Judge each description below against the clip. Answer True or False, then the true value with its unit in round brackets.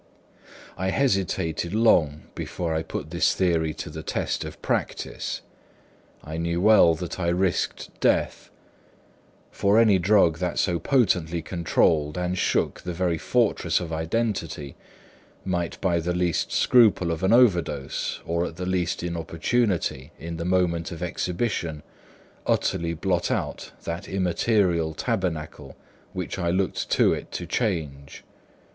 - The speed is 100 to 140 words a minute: True (135 wpm)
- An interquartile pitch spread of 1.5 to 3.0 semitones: True (2.4 semitones)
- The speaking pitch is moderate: False (85 Hz)